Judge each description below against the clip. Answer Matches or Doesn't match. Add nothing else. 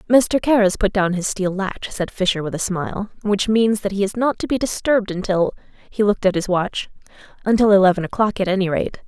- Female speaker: Matches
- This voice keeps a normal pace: Doesn't match